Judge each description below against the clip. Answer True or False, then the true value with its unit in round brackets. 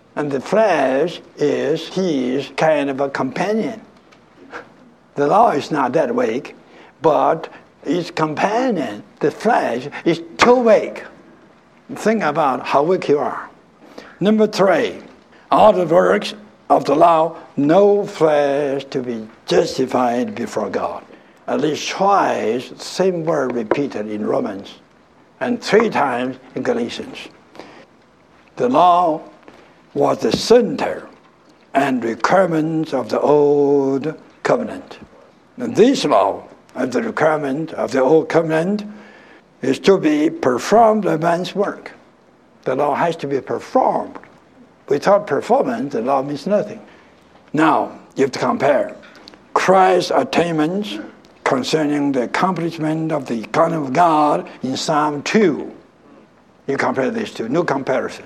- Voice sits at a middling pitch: True (160 Hz)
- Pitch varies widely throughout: True (5.9 semitones)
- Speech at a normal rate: False (125 wpm)